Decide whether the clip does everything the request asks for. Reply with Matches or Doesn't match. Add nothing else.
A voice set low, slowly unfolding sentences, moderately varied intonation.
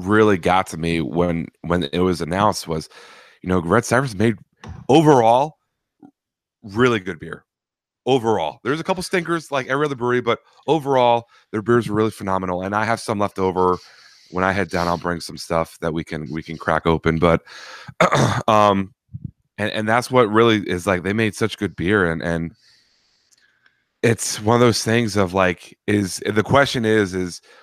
Doesn't match